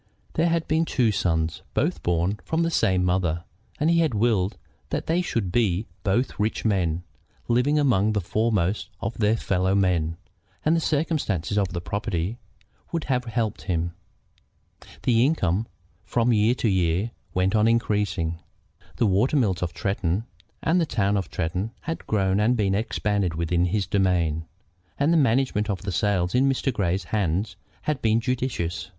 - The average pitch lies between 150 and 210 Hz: No, low, 105 Hz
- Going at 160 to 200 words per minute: Yes, average, 165 wpm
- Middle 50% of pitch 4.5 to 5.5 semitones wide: Yes, average, 4.9 semitones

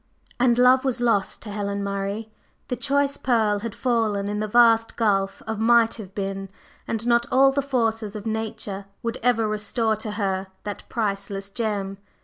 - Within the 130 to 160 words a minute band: No, average, 170 wpm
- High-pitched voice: Yes, high, 220 Hz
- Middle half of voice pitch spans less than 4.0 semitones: Yes, average, 2.9 semitones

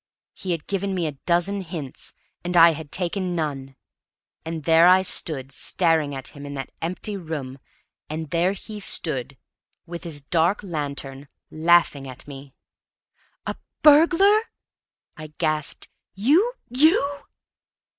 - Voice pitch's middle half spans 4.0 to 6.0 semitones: Yes, average, 4.7 semitones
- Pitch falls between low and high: Yes, medium, 165 Hz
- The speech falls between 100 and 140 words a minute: Yes, slow, 135 wpm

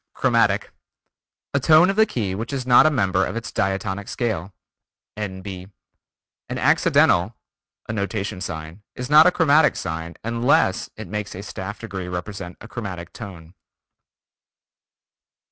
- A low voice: Yes, low, 100 Hz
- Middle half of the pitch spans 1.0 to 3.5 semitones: No, average, 4.2 semitones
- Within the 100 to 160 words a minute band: Yes, average, 140 wpm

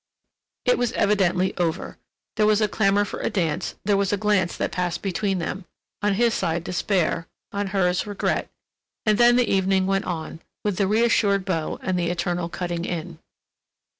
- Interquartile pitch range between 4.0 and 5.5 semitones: No, average, 2.8 semitones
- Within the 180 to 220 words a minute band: No, average, 170 wpm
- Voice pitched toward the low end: No, high, 190 Hz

